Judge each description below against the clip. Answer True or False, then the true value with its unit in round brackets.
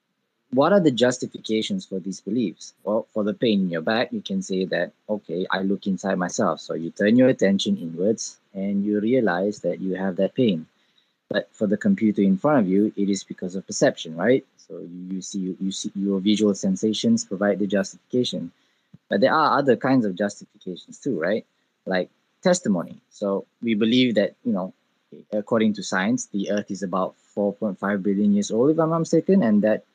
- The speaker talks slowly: False (190 wpm)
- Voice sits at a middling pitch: False (105 Hz)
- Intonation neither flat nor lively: True (3.7 semitones)